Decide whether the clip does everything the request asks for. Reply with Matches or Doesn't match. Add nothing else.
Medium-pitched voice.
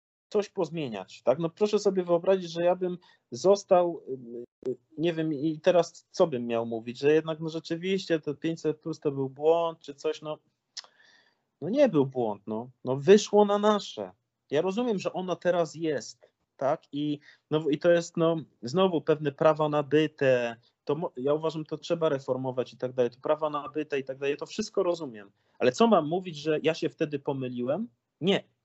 Matches